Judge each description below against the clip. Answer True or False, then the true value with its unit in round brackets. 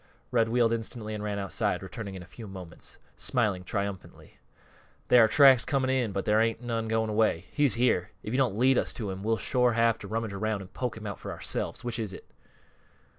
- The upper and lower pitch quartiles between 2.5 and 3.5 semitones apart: True (3.1 semitones)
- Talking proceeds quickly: True (220 wpm)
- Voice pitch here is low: True (110 Hz)